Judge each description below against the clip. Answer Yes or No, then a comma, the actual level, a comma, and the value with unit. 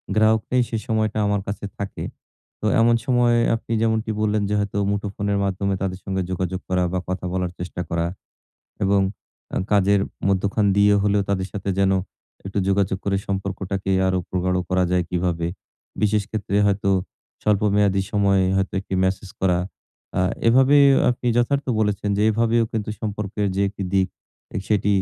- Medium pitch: No, low, 100 Hz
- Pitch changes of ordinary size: No, narrow, 2.0 semitones